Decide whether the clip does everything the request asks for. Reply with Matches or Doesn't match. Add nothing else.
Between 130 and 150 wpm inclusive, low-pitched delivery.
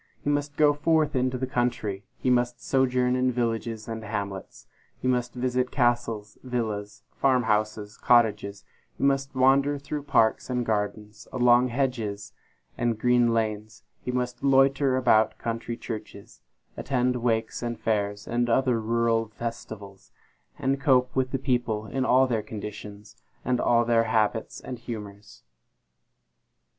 Matches